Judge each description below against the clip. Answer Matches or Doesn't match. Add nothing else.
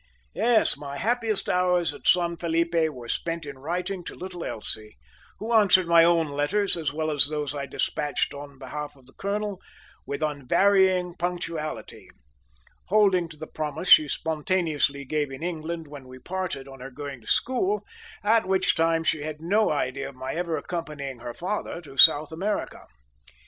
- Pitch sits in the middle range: Matches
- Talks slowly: Doesn't match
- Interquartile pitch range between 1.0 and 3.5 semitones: Doesn't match